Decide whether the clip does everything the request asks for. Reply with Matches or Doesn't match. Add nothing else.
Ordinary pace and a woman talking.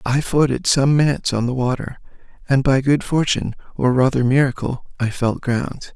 Doesn't match